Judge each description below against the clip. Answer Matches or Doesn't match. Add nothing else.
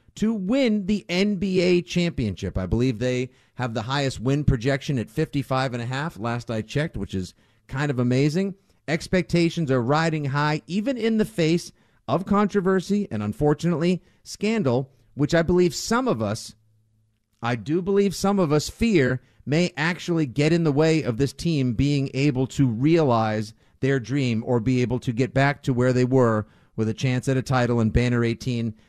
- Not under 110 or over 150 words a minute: Doesn't match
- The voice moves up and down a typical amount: Doesn't match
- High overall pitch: Doesn't match